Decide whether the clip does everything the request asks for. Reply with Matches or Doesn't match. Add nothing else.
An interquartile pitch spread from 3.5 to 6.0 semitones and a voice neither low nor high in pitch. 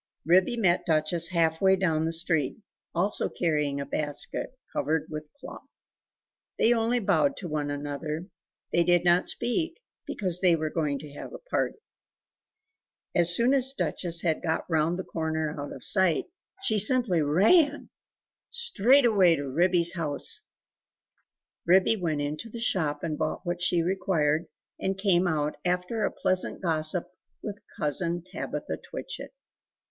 Matches